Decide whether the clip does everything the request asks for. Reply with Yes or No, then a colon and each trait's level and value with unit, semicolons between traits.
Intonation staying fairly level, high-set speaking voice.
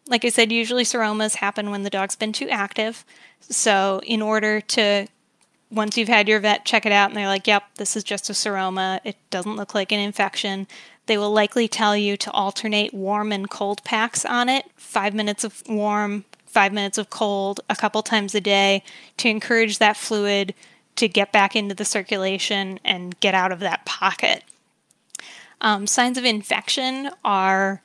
Yes: narrow, 1.7 semitones; high, 210 Hz